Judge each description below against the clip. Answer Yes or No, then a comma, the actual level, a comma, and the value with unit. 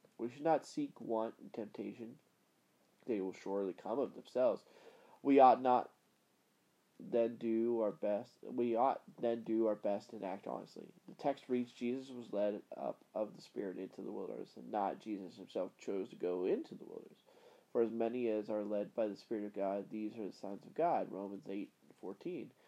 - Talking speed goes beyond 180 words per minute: Yes, average, 195 wpm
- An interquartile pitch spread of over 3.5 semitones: No, average, 3.2 semitones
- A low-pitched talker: Yes, low, 115 Hz